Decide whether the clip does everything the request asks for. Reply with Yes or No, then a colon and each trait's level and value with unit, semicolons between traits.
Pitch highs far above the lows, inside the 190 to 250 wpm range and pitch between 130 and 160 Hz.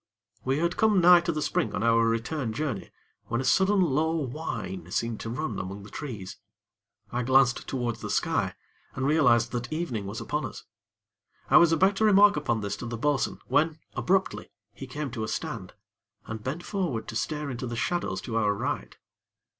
Yes: wide, 5.8 semitones; average, 195 wpm; low, 135 Hz